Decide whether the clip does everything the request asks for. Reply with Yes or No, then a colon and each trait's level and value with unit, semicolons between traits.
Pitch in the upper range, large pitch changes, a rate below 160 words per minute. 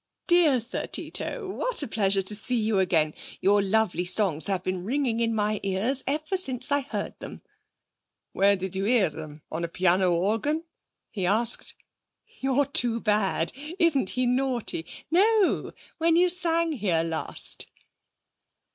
Yes: high, 220 Hz; wide, 7.1 semitones; average, 150 wpm